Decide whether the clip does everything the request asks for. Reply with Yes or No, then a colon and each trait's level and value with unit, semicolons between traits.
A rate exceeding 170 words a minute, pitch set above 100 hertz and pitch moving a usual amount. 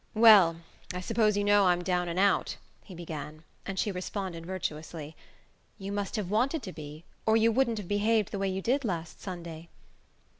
Yes: average, 185 wpm; high, 190 Hz; average, 3.7 semitones